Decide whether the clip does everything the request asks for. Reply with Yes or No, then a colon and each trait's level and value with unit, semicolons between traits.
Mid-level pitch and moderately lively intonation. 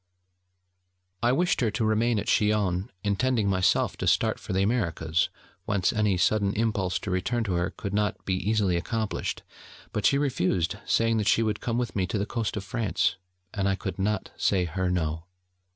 No: low, 100 Hz; average, 3.0 semitones